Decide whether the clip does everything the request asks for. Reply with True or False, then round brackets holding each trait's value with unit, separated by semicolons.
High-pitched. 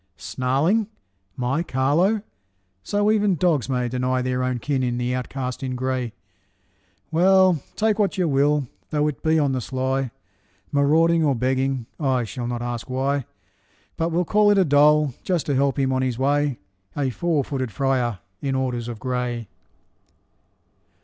False (135 Hz)